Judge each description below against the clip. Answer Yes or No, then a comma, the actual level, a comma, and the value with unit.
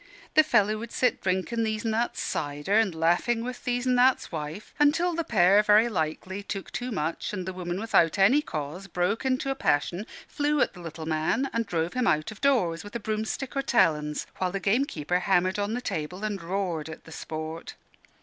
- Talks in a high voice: Yes, high, 200 Hz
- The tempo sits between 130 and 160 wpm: No, average, 200 wpm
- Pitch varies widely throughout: Yes, wide, 6.0 semitones